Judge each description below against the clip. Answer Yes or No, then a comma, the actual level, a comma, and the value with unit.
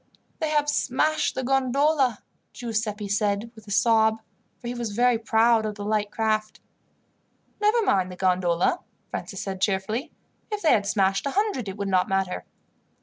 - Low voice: No, high, 220 Hz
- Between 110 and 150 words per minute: No, average, 165 wpm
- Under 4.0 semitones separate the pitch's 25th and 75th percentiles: No, average, 4.4 semitones